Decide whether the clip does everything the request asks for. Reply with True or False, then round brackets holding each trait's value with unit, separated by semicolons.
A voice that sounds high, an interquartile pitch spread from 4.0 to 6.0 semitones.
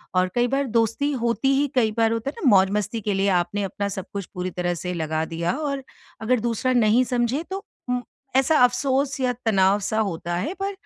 True (225 Hz; 5.3 semitones)